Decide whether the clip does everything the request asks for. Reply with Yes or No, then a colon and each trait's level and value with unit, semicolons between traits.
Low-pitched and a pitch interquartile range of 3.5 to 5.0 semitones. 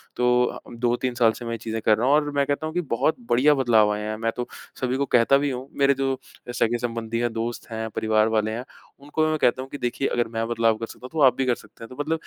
No: low, 120 Hz; average, 3.1 semitones